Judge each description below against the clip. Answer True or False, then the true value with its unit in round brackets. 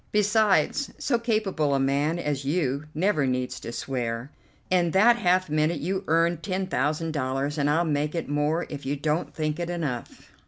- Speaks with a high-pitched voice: False (155 Hz)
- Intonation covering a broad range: False (4.3 semitones)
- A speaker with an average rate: True (175 wpm)